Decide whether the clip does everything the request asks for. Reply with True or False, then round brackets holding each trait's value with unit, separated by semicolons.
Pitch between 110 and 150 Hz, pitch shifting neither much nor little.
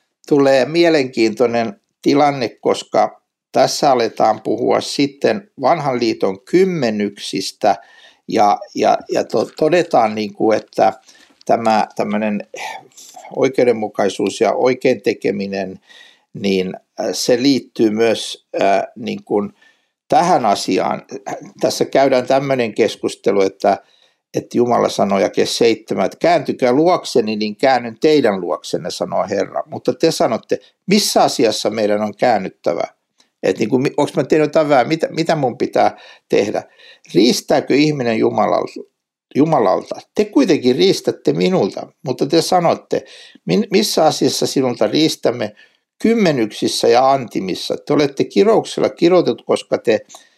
False (135 Hz; 7.6 semitones)